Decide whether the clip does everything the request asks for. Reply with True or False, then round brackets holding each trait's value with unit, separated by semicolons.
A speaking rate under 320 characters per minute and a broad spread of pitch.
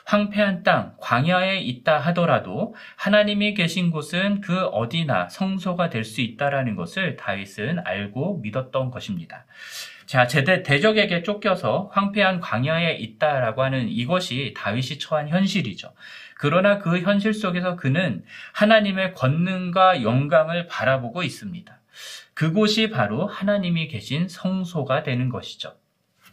True (295 characters per minute; 6.6 semitones)